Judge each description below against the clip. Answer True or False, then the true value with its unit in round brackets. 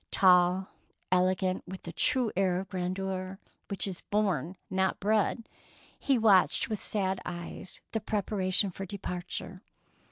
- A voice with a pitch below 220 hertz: True (190 Hz)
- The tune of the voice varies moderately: False (1.7 semitones)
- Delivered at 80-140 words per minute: True (135 wpm)